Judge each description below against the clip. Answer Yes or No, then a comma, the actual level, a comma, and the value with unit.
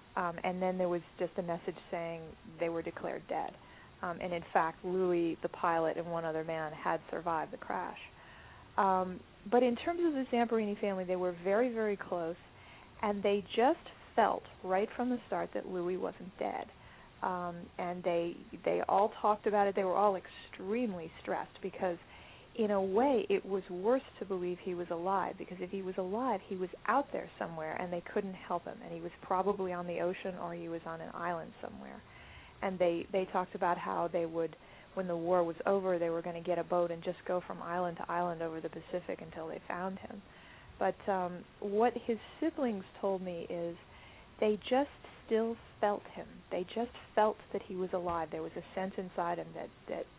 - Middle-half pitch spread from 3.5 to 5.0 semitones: No, average, 3.0 semitones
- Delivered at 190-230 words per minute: Yes, average, 200 wpm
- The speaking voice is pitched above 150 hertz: Yes, medium, 185 Hz